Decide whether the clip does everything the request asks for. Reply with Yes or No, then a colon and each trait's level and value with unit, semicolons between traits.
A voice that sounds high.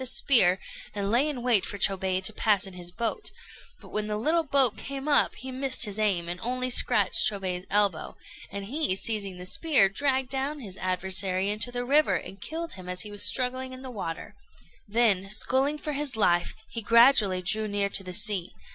Yes: high, 215 Hz